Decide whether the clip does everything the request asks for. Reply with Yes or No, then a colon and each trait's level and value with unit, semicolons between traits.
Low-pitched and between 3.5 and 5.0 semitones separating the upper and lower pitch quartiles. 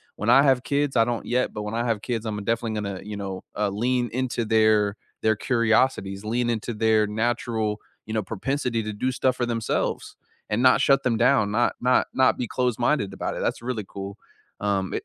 No: low, 115 Hz; average, 2.8 semitones